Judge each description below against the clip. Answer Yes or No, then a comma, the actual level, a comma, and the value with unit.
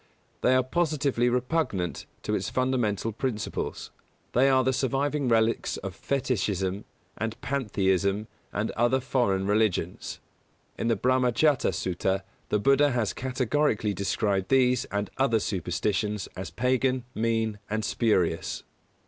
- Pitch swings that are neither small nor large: Yes, average, 4.3 semitones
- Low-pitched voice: Yes, low, 115 Hz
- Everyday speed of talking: No, slow, 125 wpm